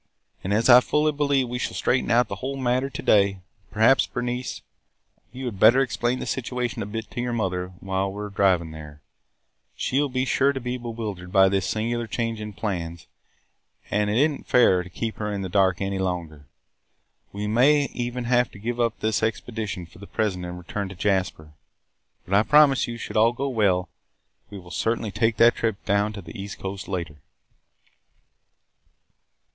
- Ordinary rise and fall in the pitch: Yes, average, 4.2 semitones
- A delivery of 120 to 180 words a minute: No, average, 190 wpm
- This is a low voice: Yes, low, 110 Hz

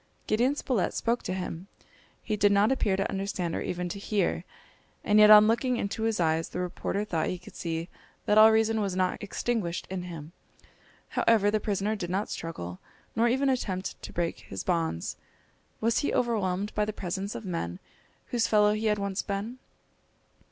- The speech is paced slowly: No, average, 185 wpm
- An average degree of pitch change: Yes, average, 3.4 semitones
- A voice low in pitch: No, high, 200 Hz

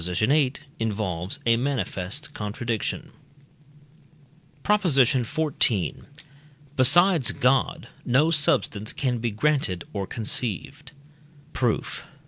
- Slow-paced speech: Yes, slow, 85 wpm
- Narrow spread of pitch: No, wide, 5.6 semitones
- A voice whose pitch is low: Yes, low, 125 Hz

